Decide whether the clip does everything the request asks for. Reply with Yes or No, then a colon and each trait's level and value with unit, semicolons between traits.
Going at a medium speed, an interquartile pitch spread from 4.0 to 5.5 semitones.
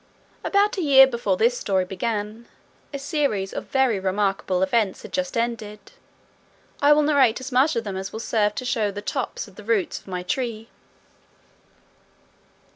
Yes: average, 170 wpm; average, 4.8 semitones